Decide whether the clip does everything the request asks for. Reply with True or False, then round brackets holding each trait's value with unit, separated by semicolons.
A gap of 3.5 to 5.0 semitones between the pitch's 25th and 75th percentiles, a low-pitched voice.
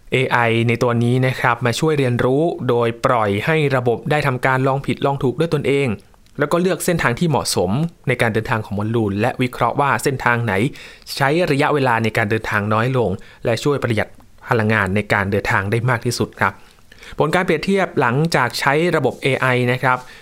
True (3.8 semitones; 125 Hz)